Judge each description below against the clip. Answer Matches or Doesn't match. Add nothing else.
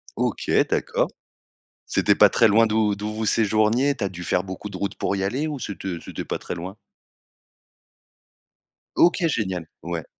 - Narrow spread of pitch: Doesn't match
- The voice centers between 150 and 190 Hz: Doesn't match